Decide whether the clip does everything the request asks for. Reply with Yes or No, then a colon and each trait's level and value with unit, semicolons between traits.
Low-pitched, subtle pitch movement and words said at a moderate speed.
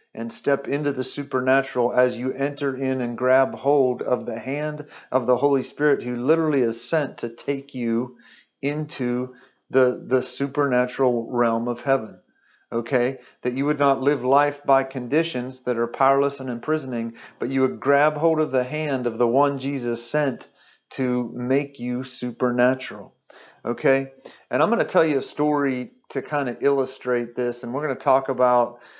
Yes: low, 130 Hz; narrow, 2.3 semitones; average, 170 wpm